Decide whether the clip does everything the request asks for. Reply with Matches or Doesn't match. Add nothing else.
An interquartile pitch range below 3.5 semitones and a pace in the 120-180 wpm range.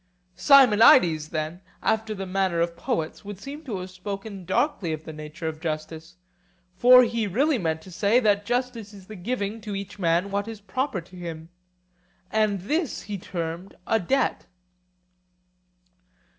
Doesn't match